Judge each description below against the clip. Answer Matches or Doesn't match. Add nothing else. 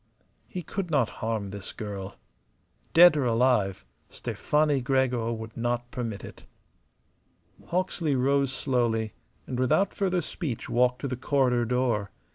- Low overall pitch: Matches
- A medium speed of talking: Doesn't match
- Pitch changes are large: Doesn't match